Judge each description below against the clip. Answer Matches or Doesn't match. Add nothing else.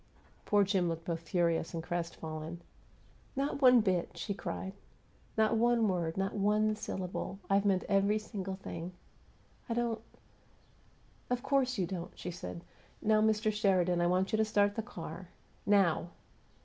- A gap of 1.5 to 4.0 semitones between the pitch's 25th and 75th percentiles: Matches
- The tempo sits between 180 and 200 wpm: Doesn't match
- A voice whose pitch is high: Matches